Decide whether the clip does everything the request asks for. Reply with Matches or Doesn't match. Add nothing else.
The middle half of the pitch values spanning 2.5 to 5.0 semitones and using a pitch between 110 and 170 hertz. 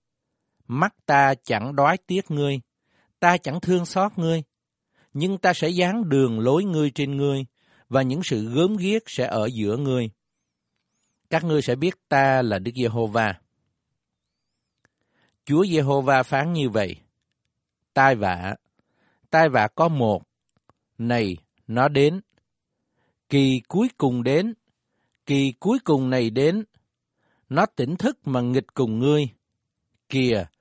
Doesn't match